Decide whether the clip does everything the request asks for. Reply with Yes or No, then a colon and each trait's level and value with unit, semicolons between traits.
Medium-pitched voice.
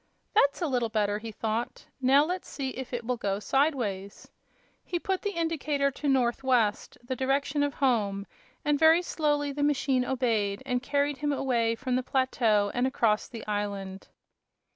No: very high, 260 Hz